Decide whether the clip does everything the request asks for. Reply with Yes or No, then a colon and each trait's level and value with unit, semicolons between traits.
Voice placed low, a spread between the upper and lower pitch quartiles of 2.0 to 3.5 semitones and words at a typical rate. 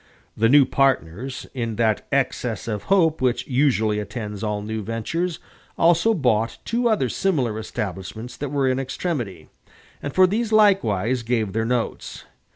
No: low, 125 Hz; average, 5.3 semitones; average, 150 wpm